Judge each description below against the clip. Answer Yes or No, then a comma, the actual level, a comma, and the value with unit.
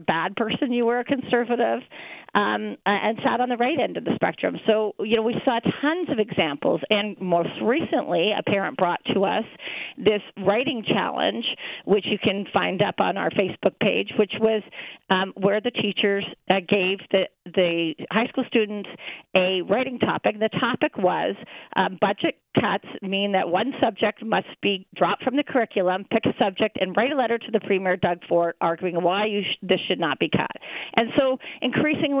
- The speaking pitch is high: Yes, high, 210 Hz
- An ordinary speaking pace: Yes, average, 185 wpm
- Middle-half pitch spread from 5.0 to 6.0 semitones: No, average, 4.2 semitones